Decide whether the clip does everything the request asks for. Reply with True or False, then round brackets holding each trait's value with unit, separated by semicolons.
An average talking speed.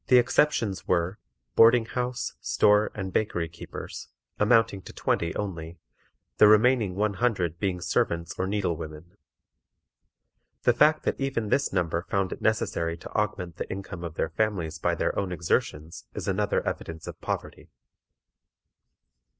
True (145 wpm)